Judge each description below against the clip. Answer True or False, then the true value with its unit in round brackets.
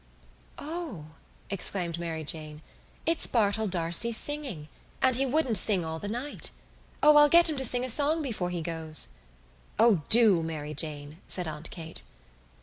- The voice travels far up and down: True (8.3 semitones)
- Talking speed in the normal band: True (155 wpm)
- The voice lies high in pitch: True (195 Hz)